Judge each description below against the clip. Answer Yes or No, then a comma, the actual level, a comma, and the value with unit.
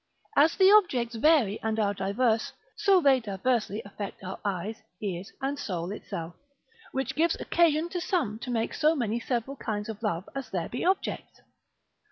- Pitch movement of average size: No, wide, 6.0 semitones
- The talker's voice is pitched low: No, high, 230 Hz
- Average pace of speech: Yes, average, 170 wpm